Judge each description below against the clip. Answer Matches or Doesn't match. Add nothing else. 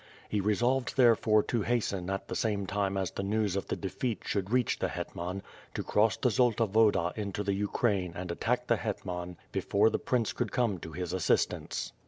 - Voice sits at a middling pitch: Doesn't match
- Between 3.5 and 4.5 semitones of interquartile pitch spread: Doesn't match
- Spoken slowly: Doesn't match